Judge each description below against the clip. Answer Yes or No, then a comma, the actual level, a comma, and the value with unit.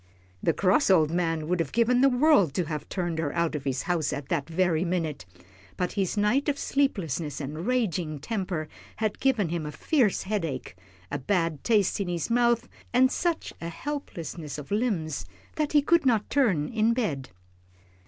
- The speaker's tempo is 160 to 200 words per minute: Yes, average, 180 wpm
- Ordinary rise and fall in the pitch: No, wide, 7.1 semitones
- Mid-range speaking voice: Yes, medium, 180 Hz